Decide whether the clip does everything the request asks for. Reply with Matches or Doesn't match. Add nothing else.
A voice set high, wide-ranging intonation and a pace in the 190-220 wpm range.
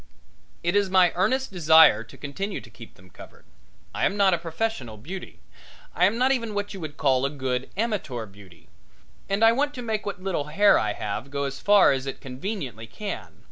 Doesn't match